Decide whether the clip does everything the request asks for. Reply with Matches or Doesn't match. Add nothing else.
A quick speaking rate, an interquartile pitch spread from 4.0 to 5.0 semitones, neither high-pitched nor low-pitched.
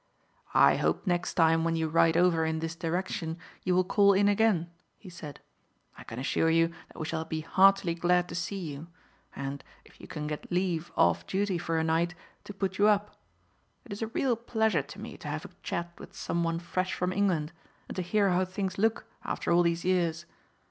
Doesn't match